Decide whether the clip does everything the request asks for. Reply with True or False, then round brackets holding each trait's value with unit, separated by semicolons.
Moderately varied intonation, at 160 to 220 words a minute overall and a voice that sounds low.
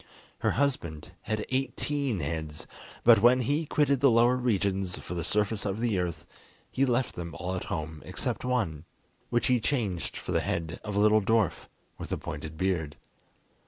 False (6.5 semitones; 175 wpm; 105 Hz)